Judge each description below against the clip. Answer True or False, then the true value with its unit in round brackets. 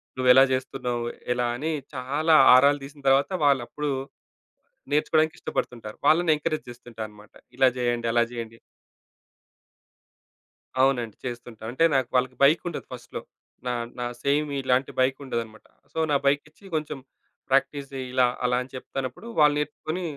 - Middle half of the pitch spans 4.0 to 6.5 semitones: False (3.2 semitones)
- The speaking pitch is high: False (130 Hz)